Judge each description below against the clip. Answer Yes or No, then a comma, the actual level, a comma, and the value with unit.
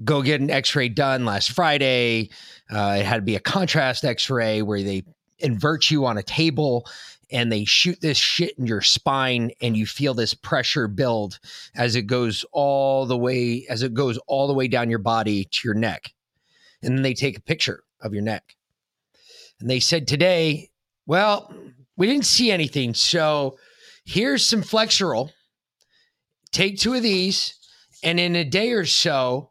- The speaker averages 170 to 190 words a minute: Yes, average, 180 wpm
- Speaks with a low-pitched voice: Yes, low, 130 Hz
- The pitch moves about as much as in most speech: No, wide, 5.8 semitones